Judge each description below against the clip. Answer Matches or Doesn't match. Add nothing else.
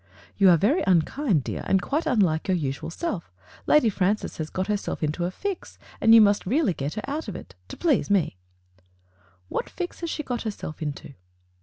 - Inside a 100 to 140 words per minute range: Doesn't match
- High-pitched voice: Matches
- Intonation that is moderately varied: Doesn't match